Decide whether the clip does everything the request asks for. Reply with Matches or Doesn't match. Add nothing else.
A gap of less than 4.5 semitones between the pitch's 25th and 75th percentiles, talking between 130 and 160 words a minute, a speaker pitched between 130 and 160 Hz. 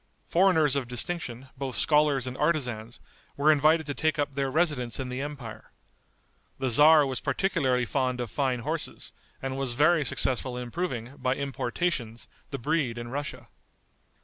Matches